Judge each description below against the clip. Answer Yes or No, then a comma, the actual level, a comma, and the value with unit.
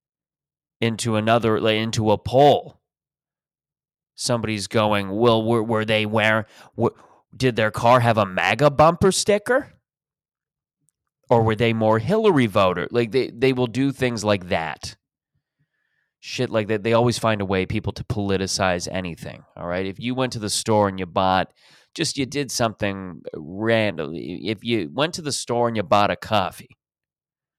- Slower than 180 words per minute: Yes, average, 165 wpm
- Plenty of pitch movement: No, average, 3.8 semitones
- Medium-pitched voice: No, low, 115 Hz